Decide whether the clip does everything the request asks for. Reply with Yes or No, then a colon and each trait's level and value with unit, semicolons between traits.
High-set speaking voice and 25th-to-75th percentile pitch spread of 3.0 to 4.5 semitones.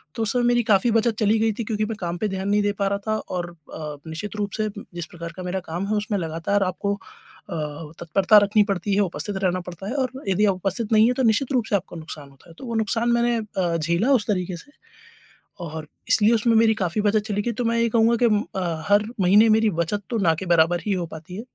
Yes: high, 205 Hz; average, 4.1 semitones